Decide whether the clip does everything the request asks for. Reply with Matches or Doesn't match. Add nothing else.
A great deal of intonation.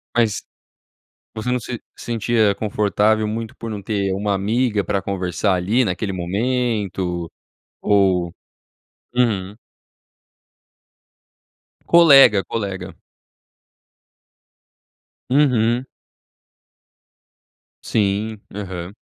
Doesn't match